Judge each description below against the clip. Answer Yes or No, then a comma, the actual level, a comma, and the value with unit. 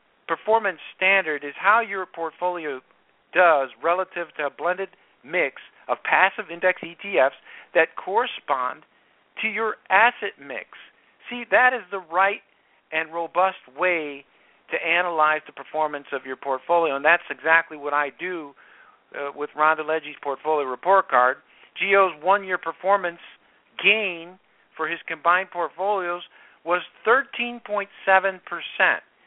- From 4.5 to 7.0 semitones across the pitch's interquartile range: No, average, 3.9 semitones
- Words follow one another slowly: Yes, slow, 125 wpm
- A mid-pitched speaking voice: Yes, medium, 175 Hz